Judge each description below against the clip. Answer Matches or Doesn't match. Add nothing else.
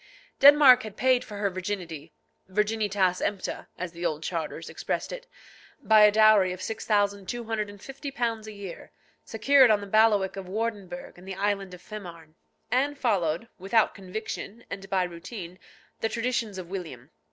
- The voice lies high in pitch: Matches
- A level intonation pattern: Doesn't match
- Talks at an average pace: Matches